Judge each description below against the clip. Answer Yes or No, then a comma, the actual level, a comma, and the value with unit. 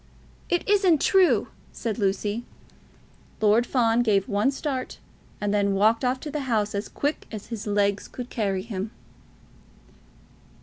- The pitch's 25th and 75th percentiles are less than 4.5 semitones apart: Yes, average, 4.1 semitones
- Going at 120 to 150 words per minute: Yes, average, 140 wpm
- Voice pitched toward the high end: Yes, high, 225 Hz